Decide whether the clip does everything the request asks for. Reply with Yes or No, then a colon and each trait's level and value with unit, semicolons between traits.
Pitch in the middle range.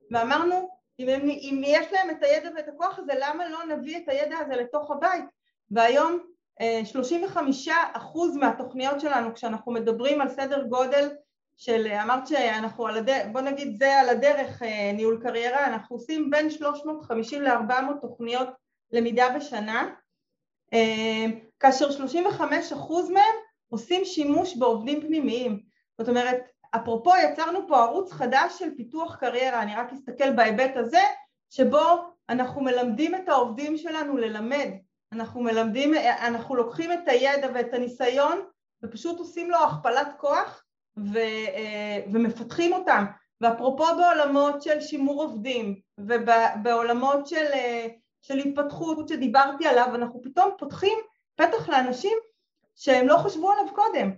No: very high, 275 Hz